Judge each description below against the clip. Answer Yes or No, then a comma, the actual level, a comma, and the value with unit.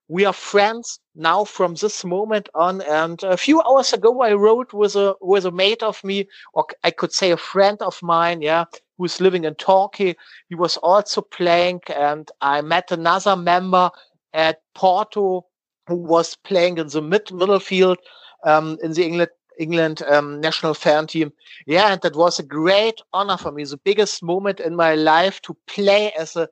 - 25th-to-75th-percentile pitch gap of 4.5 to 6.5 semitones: No, average, 3.3 semitones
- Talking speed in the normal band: Yes, average, 190 wpm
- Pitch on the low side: No, medium, 180 Hz